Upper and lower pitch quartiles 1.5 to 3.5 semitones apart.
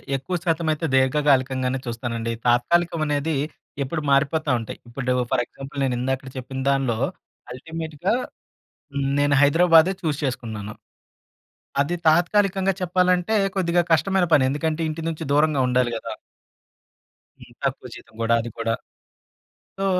No: average, 4.4 semitones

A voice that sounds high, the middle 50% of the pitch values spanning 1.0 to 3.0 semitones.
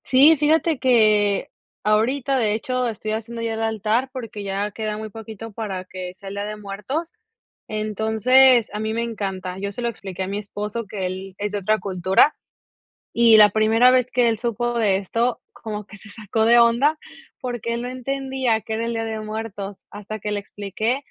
Yes: high, 220 Hz; narrow, 2.5 semitones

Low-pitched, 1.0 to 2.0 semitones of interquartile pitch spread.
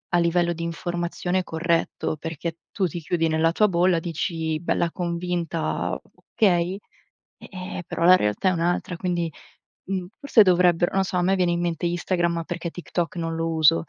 No: medium, 175 Hz; narrow, 1.4 semitones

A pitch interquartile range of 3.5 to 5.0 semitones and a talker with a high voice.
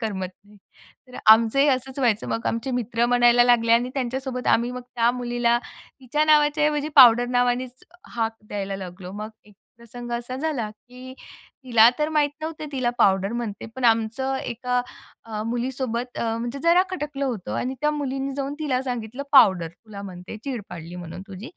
No: average, 3.0 semitones; high, 240 Hz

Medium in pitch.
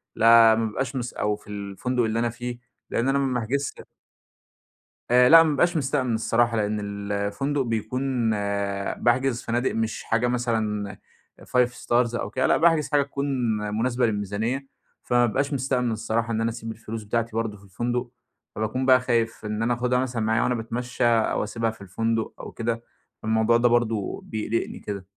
No: low, 115 Hz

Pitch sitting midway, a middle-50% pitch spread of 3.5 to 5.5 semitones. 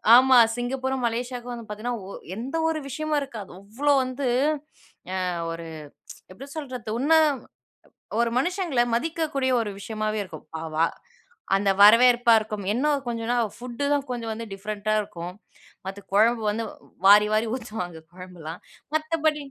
No: high, 235 Hz; average, 4.0 semitones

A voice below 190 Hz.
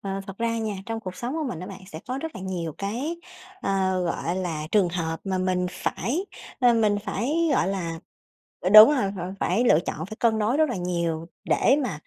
No: high, 195 Hz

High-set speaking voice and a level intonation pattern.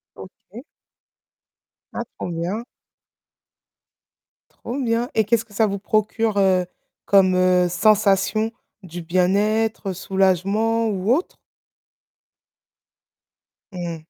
No: high, 200 Hz; average, 3.3 semitones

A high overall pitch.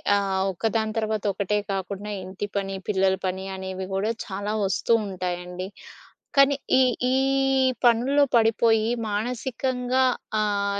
Yes: high, 205 Hz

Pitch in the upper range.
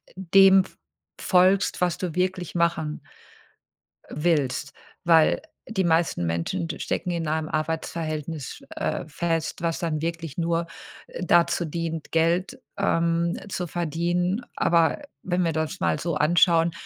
No: medium, 170 Hz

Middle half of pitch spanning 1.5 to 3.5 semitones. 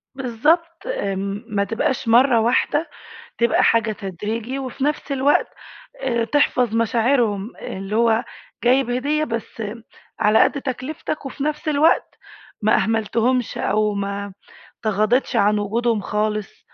No: average, 4.0 semitones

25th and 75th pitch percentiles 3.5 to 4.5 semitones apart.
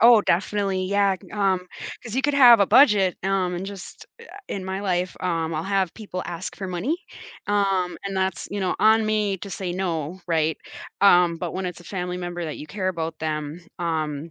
No: narrow, 2.5 semitones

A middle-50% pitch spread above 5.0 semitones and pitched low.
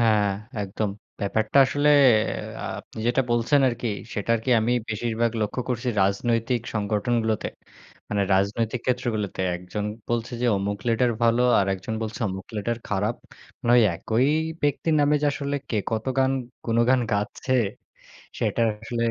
No: average, 2.8 semitones; low, 115 Hz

